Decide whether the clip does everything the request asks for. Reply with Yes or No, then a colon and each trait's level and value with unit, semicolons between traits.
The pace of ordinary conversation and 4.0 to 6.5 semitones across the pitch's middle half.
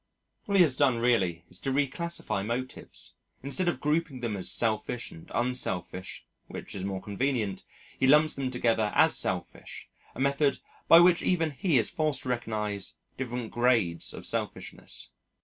Yes: average, 160 wpm; average, 5.2 semitones